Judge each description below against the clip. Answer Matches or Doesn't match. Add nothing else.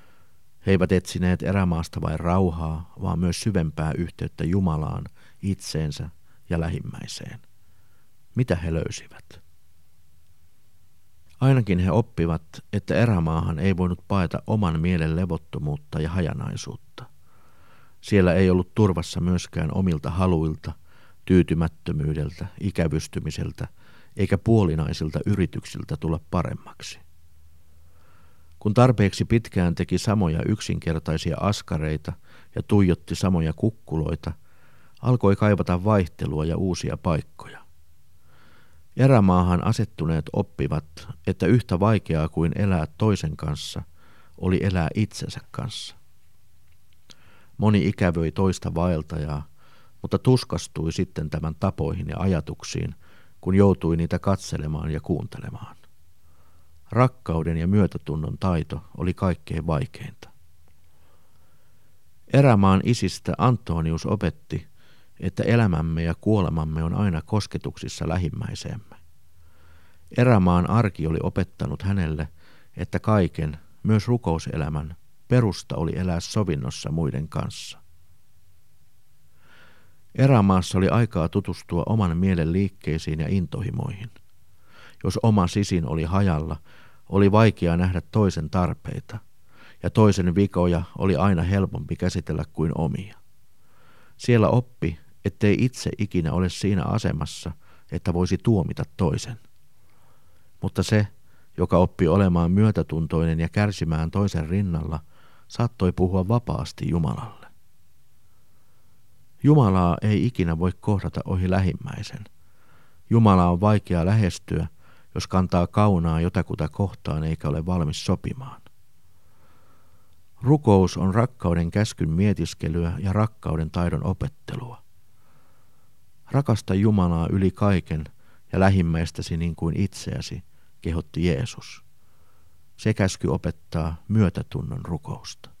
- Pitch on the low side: Matches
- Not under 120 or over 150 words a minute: Doesn't match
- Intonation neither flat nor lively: Matches